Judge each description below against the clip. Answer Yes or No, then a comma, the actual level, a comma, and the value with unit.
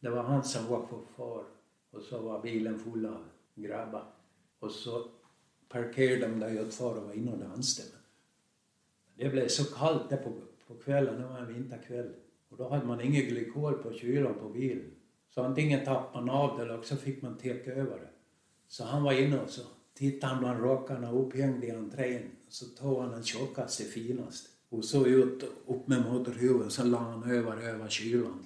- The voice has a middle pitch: No, low, 125 Hz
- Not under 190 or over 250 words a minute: Yes, average, 195 wpm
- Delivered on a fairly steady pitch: Yes, narrow, 2.3 semitones